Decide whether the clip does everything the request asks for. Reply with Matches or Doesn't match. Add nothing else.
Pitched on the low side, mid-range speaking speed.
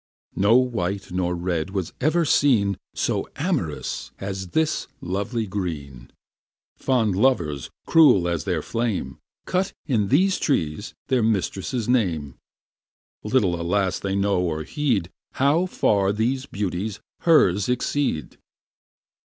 Doesn't match